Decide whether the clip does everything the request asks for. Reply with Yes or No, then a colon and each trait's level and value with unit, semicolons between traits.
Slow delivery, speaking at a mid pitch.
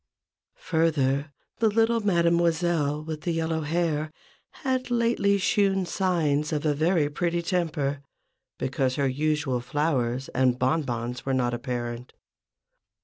Yes: slow, 120 wpm; medium, 155 Hz